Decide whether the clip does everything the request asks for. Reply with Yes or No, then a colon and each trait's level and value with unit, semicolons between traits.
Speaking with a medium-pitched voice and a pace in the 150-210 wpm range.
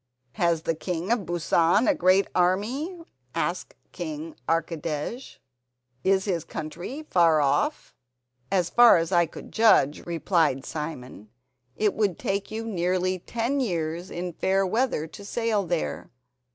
No: medium, 180 Hz; slow, 135 wpm